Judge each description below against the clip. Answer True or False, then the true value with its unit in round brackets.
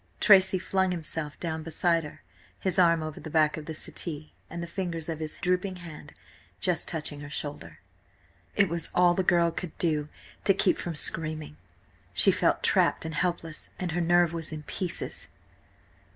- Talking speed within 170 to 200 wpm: True (175 wpm)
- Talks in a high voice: False (165 Hz)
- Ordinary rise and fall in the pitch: False (2.3 semitones)